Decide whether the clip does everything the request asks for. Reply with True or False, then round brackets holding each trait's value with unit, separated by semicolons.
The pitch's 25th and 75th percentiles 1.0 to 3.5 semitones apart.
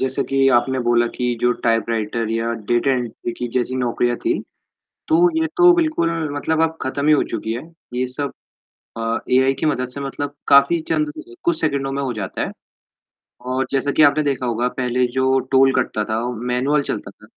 True (2.8 semitones)